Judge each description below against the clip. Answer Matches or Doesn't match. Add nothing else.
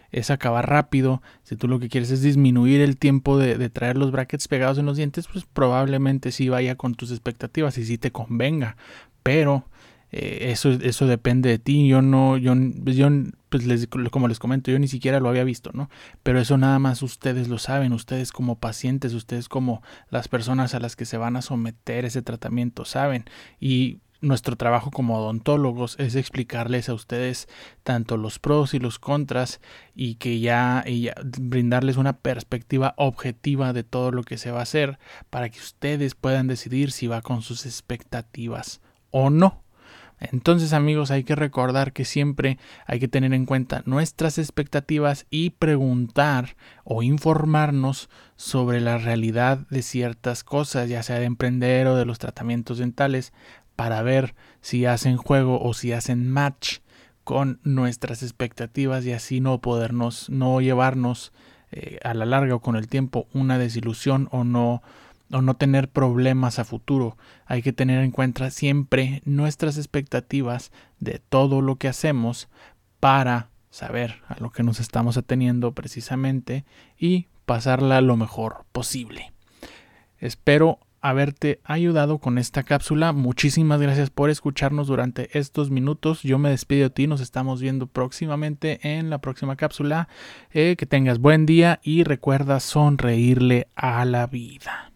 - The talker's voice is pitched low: Matches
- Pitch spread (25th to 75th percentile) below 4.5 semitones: Matches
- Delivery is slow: Doesn't match